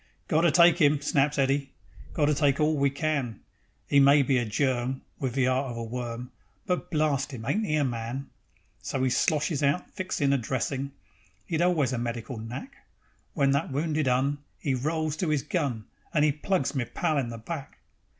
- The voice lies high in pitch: No, medium, 140 Hz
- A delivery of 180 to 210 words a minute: Yes, average, 195 wpm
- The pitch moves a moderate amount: Yes, average, 3.1 semitones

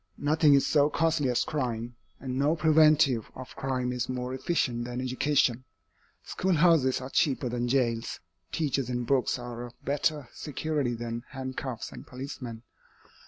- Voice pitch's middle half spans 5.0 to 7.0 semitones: No, average, 3.3 semitones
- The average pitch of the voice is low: Yes, low, 130 Hz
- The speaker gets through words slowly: No, average, 145 wpm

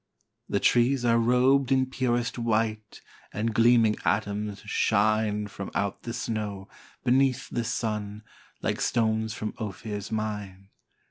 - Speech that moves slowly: Yes, slow, 125 wpm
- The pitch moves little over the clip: Yes, narrow, 2.3 semitones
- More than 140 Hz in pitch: No, low, 110 Hz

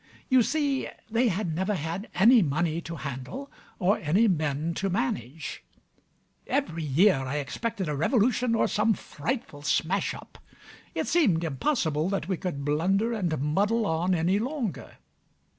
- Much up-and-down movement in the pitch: Yes, wide, 6.5 semitones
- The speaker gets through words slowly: No, average, 145 wpm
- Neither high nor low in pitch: Yes, medium, 180 Hz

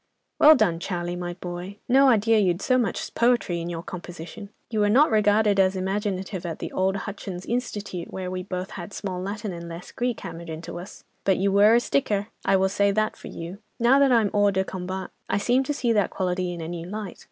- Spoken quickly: Yes, fast, 220 wpm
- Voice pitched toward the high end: Yes, high, 195 Hz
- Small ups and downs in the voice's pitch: No, average, 3.3 semitones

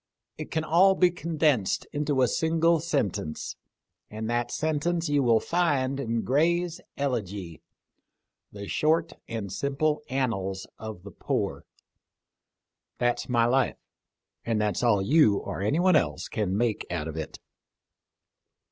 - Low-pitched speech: Yes, low, 130 Hz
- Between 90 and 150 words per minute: Yes, slow, 135 wpm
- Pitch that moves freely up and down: Yes, wide, 6.9 semitones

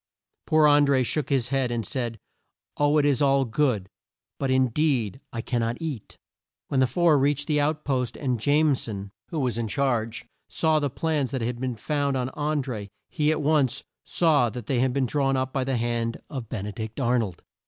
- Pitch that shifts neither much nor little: Yes, average, 3.6 semitones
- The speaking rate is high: Yes, fast, 215 wpm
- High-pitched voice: No, low, 130 Hz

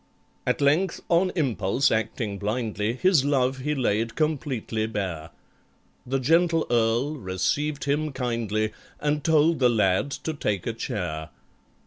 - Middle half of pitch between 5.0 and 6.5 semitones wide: Yes, wide, 5.6 semitones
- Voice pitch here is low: Yes, low, 125 Hz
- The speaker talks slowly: Yes, slow, 130 wpm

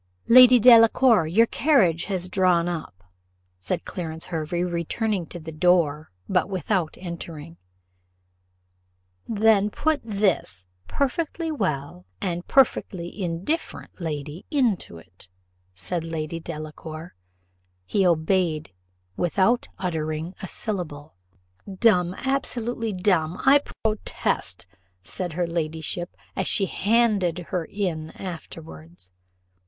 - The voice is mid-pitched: Yes, medium, 175 Hz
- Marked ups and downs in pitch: No, average, 4.8 semitones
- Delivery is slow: Yes, slow, 105 wpm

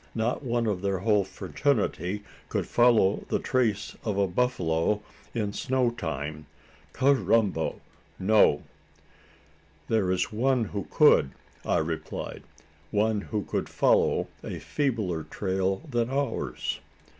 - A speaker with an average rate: No, slow, 120 wpm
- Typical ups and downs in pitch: Yes, average, 4.2 semitones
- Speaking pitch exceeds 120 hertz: No, low, 105 Hz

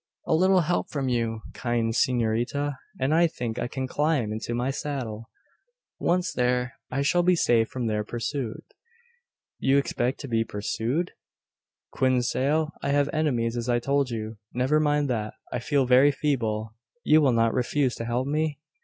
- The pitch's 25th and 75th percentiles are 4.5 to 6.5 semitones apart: No, average, 3.9 semitones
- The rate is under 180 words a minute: Yes, average, 170 wpm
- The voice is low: Yes, low, 130 Hz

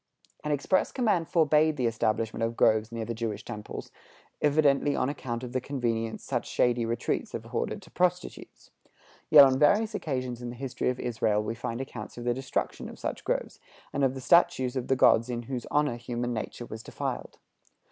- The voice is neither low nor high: No, low, 125 Hz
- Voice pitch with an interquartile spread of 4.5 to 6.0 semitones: No, average, 3.7 semitones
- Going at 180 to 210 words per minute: Yes, average, 190 wpm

